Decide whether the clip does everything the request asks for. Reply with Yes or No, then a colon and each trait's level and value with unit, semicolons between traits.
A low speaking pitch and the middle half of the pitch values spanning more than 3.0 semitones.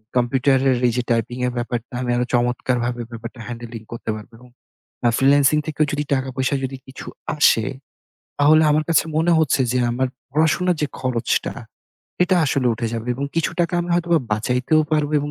Yes: low, 130 Hz; average, 3.9 semitones